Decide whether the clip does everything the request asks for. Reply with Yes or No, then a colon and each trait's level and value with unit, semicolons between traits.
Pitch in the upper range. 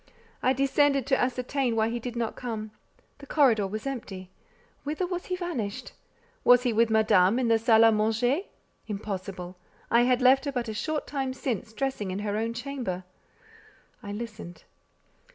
Yes: high, 235 Hz